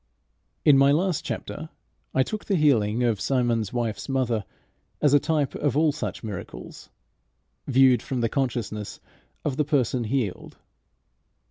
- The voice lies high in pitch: No, low, 130 Hz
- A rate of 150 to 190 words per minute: No, average, 140 wpm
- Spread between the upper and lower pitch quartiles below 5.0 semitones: Yes, average, 3.9 semitones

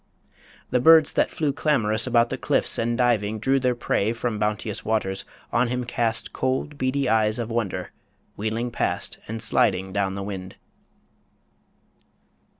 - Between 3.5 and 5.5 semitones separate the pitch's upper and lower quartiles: No, average, 3.0 semitones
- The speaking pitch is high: No, low, 115 Hz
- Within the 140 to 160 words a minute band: Yes, average, 150 wpm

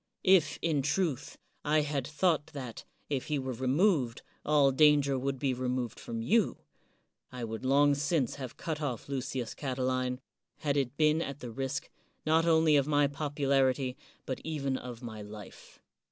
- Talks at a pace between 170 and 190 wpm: No, average, 160 wpm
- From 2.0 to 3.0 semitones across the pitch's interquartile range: Yes, average, 2.7 semitones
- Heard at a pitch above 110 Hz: Yes, medium, 140 Hz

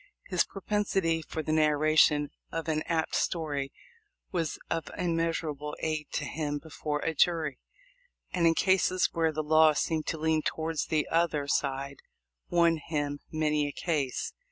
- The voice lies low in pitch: No, medium, 155 Hz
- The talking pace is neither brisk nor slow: Yes, average, 155 wpm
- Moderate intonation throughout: No, narrow, 1.8 semitones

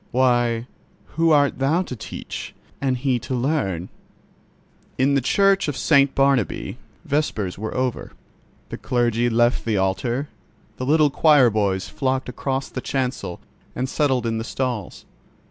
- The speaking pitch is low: Yes, low, 130 Hz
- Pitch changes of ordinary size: Yes, average, 3.1 semitones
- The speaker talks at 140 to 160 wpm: Yes, average, 145 wpm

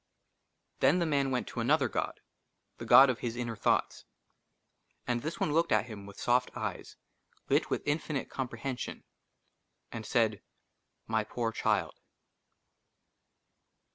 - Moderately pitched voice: No, low, 125 Hz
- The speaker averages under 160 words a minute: Yes, average, 140 wpm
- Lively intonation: No, average, 3.6 semitones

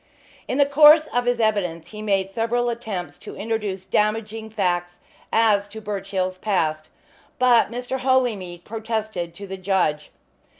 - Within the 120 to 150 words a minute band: Yes, average, 140 wpm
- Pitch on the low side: No, high, 210 Hz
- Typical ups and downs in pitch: Yes, average, 3.8 semitones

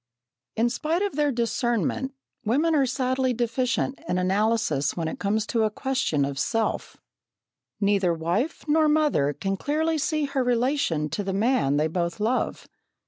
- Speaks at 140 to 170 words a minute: Yes, average, 155 wpm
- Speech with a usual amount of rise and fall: No, wide, 6.1 semitones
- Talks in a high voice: Yes, high, 235 Hz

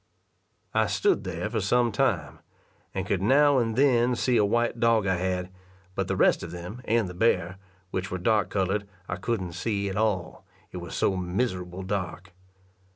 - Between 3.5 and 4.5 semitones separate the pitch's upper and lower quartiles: Yes, average, 4.2 semitones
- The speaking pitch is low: Yes, low, 100 Hz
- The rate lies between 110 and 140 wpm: No, average, 180 wpm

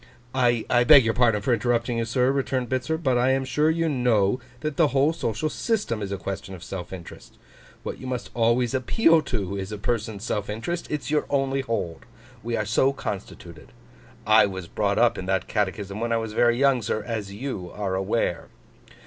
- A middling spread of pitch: Yes, average, 4.6 semitones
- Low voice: Yes, low, 115 Hz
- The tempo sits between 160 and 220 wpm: Yes, average, 200 wpm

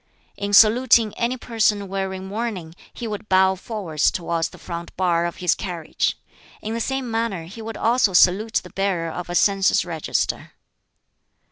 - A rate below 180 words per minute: Yes, average, 160 wpm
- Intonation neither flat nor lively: Yes, average, 4.1 semitones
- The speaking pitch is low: No, high, 195 Hz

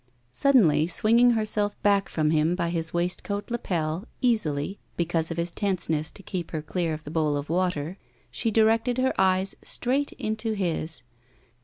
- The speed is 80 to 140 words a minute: No, average, 160 wpm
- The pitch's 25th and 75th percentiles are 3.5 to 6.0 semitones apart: Yes, average, 5.2 semitones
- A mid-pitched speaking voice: Yes, medium, 180 Hz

